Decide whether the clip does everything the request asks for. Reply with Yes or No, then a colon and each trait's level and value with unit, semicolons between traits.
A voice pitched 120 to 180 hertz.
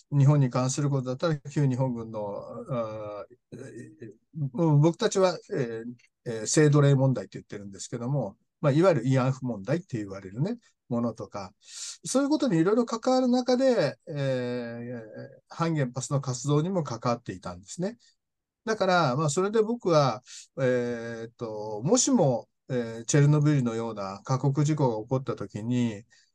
Yes: low, 135 Hz